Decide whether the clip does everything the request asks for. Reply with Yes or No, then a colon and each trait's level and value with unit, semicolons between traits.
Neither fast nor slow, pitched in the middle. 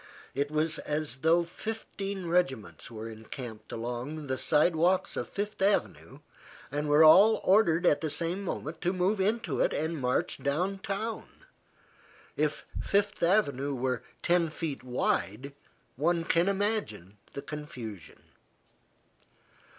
No: slow, 125 wpm; medium, 160 Hz